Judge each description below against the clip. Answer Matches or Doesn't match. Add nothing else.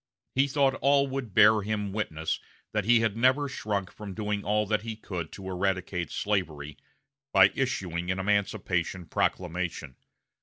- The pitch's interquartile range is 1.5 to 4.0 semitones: Matches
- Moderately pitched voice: Doesn't match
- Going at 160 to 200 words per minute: Doesn't match